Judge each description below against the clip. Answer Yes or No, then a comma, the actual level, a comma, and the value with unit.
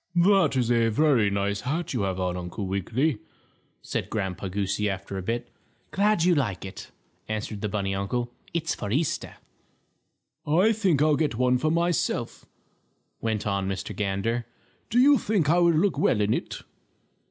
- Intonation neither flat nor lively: No, wide, 8.3 semitones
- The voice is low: Yes, low, 120 Hz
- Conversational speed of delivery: Yes, average, 165 wpm